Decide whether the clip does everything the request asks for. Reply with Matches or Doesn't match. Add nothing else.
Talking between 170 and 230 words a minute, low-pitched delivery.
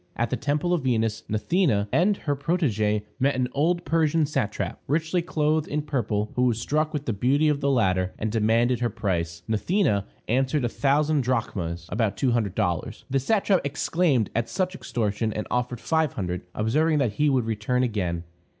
Matches